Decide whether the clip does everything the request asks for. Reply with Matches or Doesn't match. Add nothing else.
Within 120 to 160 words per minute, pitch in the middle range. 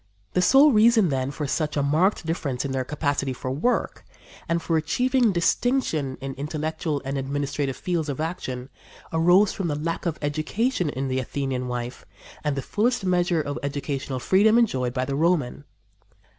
Doesn't match